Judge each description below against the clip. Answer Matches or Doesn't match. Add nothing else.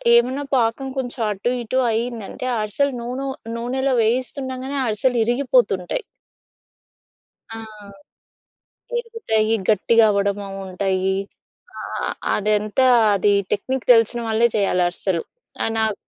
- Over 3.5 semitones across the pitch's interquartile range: Matches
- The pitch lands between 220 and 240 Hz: Matches